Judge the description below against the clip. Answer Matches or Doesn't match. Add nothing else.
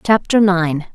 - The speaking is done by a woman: Matches